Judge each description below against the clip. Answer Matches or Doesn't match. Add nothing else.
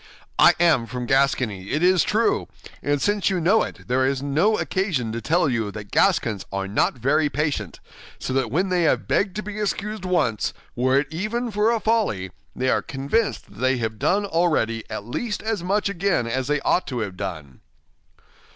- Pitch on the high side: Doesn't match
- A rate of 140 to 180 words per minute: Doesn't match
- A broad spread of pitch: Matches